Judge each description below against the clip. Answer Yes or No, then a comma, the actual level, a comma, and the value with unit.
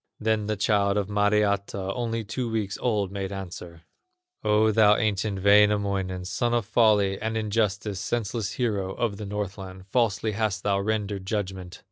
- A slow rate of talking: No, average, 150 wpm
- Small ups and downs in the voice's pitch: Yes, narrow, 2.0 semitones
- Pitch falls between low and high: No, low, 105 Hz